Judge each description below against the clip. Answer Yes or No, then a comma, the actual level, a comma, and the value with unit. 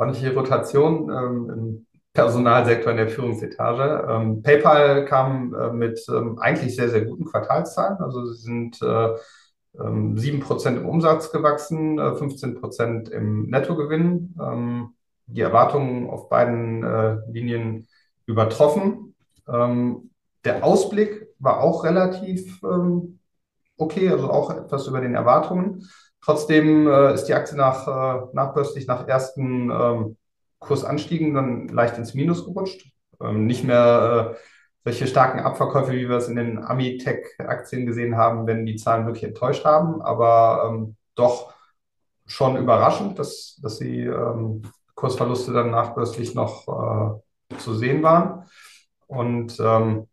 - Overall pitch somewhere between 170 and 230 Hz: No, low, 125 Hz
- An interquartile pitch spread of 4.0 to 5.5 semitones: Yes, average, 4.4 semitones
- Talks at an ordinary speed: No, slow, 120 wpm